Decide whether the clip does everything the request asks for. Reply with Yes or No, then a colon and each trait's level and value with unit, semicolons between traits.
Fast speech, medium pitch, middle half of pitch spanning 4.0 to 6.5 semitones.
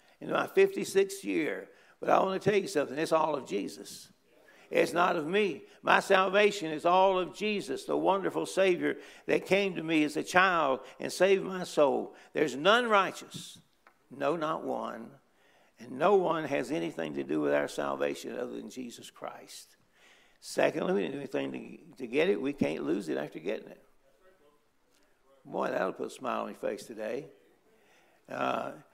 No: average, 175 wpm; medium, 180 Hz; average, 4.5 semitones